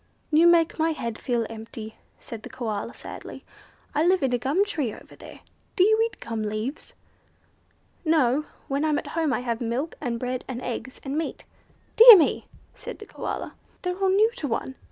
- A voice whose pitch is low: No, very high, 275 Hz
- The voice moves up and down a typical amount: No, wide, 5.8 semitones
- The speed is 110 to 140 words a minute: No, average, 190 wpm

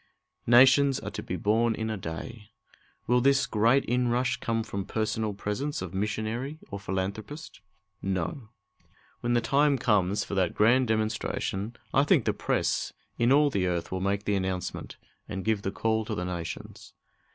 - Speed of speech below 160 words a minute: No, average, 165 wpm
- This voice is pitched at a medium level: No, low, 110 Hz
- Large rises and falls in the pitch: No, average, 3.9 semitones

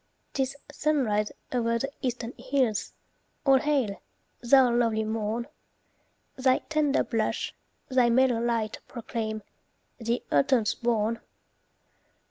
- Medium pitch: No, high, 235 Hz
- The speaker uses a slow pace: Yes, slow, 100 wpm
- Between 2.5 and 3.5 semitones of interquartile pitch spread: Yes, average, 2.9 semitones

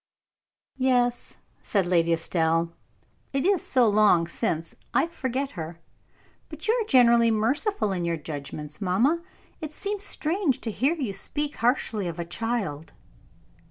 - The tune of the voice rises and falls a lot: Yes, wide, 8.4 semitones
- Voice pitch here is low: No, high, 225 Hz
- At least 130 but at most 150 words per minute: Yes, average, 140 wpm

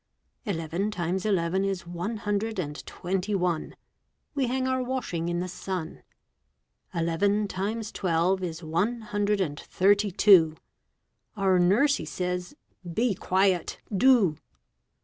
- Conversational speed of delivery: No, slow, 125 wpm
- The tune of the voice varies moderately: Yes, average, 3.3 semitones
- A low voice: No, high, 190 Hz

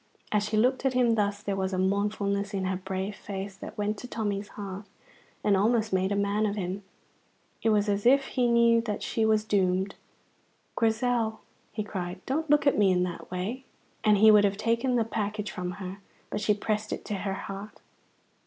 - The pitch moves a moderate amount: No, narrow, 2.3 semitones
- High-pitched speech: Yes, high, 205 Hz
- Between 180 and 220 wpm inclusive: Yes, average, 200 wpm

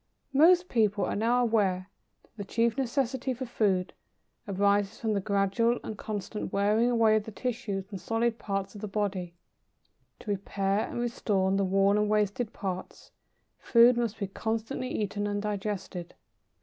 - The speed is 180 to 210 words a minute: No, average, 160 wpm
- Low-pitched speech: No, high, 210 Hz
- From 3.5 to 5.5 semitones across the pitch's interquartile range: No, average, 2.8 semitones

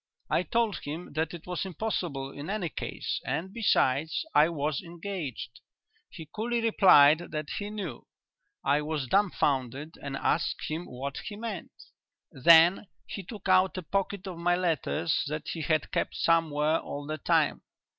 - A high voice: No, medium, 165 Hz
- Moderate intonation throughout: Yes, average, 4.2 semitones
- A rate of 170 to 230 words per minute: No, average, 155 wpm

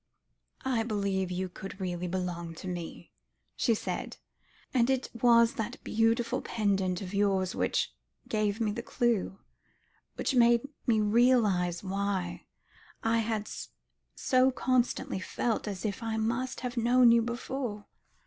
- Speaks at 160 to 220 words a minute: No, slow, 135 wpm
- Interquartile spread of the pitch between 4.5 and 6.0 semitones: No, average, 3.8 semitones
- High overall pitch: Yes, high, 220 Hz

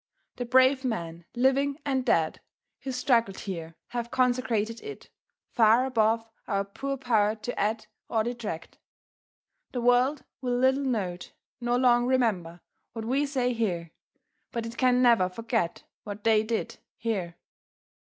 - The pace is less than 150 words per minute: Yes, average, 140 wpm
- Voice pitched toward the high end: Yes, high, 235 Hz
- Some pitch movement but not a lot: Yes, average, 3.3 semitones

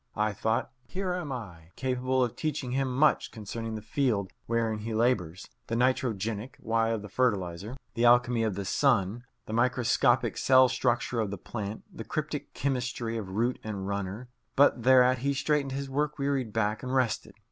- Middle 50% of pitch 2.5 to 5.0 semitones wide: Yes, average, 3.3 semitones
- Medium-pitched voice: No, low, 120 Hz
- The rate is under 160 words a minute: No, average, 175 wpm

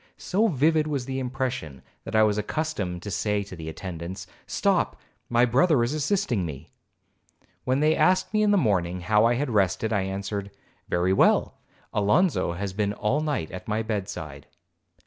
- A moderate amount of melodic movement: No, wide, 6.9 semitones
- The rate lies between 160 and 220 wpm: Yes, average, 170 wpm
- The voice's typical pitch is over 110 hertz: No, low, 105 Hz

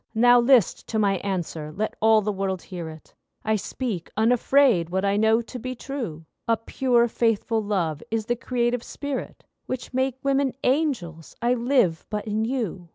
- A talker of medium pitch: No, high, 225 Hz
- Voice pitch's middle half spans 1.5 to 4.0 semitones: No, average, 4.4 semitones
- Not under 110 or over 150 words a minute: No, average, 165 wpm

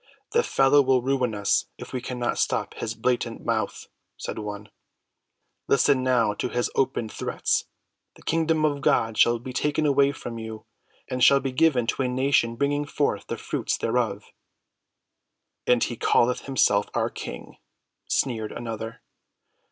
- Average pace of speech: Yes, average, 150 wpm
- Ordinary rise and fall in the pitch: Yes, average, 3.4 semitones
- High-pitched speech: No, low, 125 Hz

